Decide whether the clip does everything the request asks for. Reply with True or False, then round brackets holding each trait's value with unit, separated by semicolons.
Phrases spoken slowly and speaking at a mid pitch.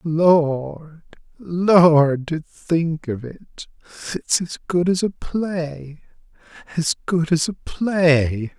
True (105 wpm; 165 Hz)